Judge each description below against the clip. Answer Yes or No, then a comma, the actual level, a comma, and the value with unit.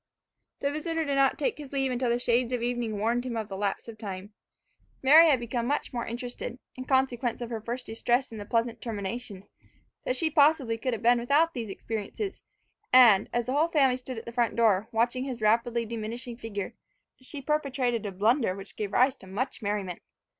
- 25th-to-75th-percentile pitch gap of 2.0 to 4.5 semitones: Yes, average, 2.8 semitones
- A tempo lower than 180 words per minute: No, fast, 205 wpm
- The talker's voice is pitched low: No, high, 240 Hz